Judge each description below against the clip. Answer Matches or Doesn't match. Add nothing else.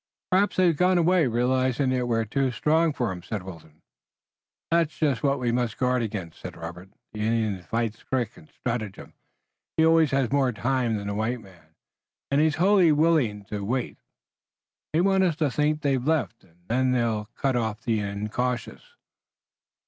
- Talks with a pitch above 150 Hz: Doesn't match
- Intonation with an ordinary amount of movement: Doesn't match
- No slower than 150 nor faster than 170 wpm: Doesn't match